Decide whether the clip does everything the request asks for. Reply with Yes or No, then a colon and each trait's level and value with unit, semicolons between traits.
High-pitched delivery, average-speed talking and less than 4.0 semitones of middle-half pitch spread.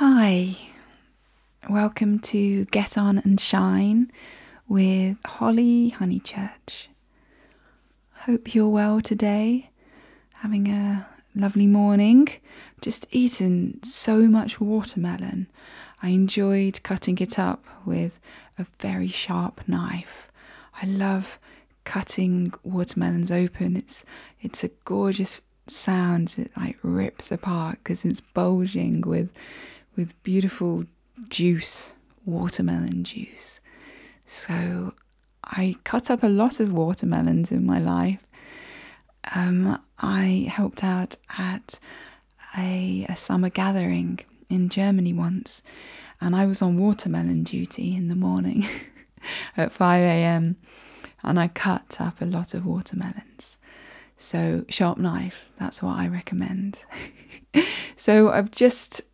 No: high, 195 Hz; slow, 110 wpm; average, 3.4 semitones